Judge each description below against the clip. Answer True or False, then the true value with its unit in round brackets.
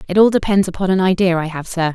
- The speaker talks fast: True (280 wpm)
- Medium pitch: True (180 Hz)